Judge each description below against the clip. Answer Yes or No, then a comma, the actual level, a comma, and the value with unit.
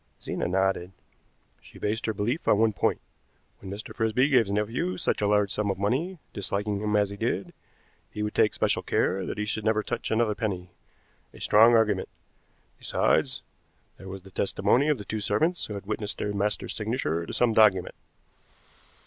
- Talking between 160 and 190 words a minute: Yes, average, 185 wpm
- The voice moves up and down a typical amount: No, narrow, 2.1 semitones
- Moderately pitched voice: No, low, 105 Hz